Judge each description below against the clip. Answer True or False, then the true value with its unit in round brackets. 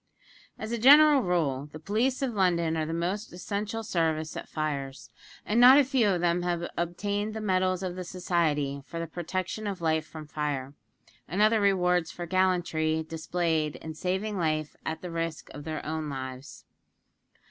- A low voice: False (175 Hz)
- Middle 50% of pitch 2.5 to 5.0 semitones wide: True (4.2 semitones)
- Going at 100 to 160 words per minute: False (180 wpm)